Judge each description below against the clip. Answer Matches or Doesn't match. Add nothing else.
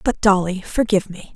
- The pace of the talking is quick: Doesn't match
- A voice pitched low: Doesn't match